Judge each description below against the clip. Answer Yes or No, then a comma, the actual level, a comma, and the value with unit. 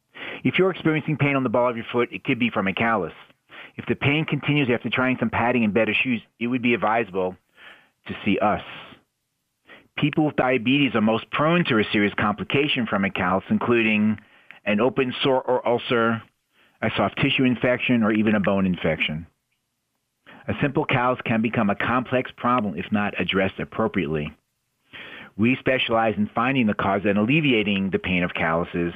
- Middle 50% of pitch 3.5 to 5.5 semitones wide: Yes, average, 4.0 semitones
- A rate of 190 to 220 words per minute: No, average, 180 wpm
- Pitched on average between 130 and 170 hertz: No, low, 115 Hz